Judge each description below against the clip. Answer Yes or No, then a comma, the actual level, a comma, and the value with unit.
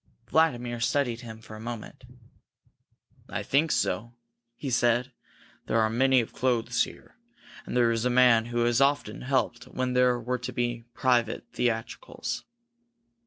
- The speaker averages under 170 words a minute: Yes, average, 150 wpm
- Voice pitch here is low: Yes, low, 120 Hz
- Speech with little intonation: Yes, narrow, 1.6 semitones